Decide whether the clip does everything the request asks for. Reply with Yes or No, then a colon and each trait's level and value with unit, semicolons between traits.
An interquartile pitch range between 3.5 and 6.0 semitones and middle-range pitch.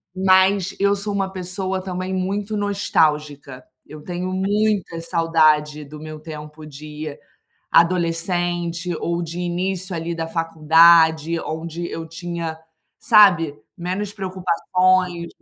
No: narrow, 2.6 semitones; medium, 170 Hz